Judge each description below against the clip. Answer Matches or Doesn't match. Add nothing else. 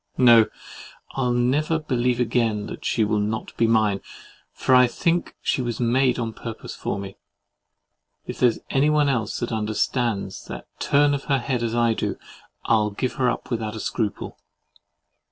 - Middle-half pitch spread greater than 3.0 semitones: Doesn't match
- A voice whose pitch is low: Matches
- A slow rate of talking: Doesn't match